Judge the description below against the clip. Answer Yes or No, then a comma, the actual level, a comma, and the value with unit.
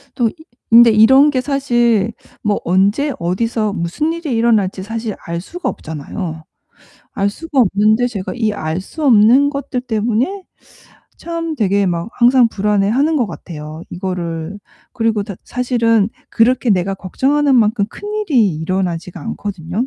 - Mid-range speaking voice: No, high, 220 Hz